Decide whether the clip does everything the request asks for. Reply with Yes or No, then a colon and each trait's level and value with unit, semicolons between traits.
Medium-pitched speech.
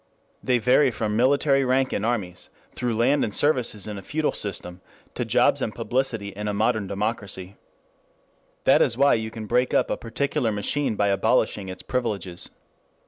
No: low, 110 Hz